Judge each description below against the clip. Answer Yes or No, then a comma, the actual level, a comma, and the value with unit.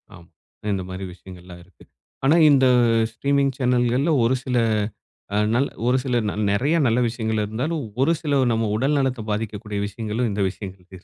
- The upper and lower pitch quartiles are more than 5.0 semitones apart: No, average, 4.6 semitones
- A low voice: Yes, low, 115 Hz